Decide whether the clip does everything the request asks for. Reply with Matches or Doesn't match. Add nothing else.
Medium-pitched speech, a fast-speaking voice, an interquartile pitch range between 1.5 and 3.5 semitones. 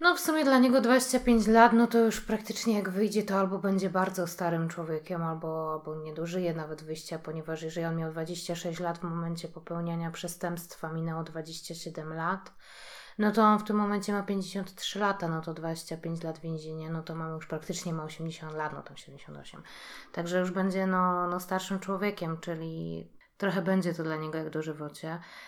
Matches